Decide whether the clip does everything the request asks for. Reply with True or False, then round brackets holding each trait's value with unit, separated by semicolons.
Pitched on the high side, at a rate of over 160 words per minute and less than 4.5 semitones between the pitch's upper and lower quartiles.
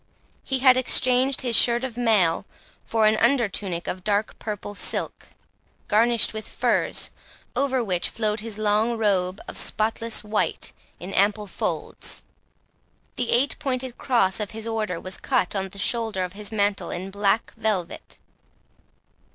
False (215 Hz; 150 wpm; 3.1 semitones)